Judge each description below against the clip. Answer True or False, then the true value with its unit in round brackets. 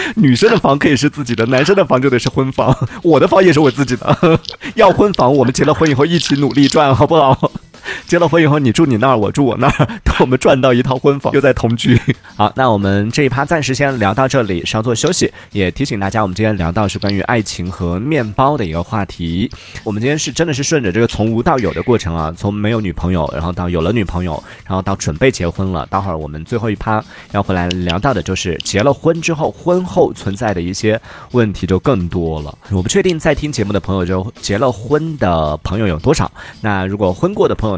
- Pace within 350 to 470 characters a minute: True (355 characters per minute)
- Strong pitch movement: True (6.6 semitones)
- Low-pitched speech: True (115 Hz)